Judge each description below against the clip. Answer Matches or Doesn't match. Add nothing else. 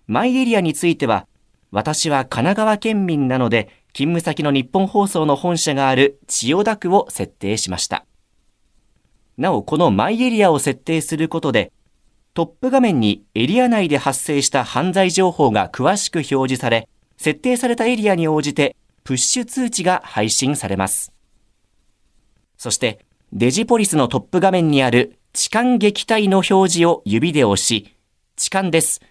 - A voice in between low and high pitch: Matches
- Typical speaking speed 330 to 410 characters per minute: Doesn't match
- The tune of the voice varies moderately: Doesn't match